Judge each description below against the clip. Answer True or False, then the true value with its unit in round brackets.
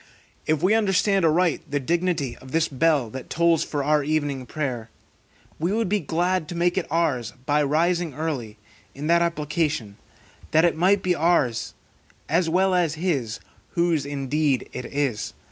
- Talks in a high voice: False (155 Hz)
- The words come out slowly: False (160 wpm)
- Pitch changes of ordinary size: True (3.7 semitones)